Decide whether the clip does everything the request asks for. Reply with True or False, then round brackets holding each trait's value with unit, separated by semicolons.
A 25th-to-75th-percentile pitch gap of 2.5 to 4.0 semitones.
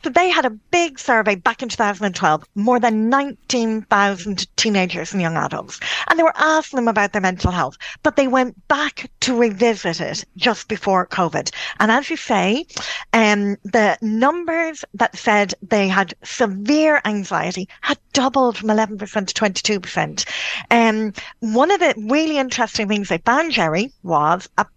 False (4.8 semitones)